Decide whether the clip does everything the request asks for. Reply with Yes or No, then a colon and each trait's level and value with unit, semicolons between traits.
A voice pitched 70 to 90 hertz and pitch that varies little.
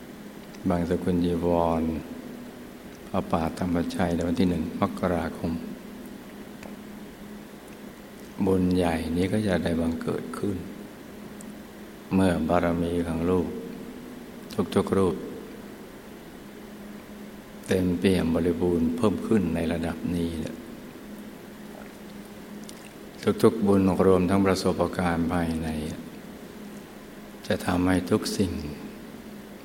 Yes: very low, 85 Hz; narrow, 1.6 semitones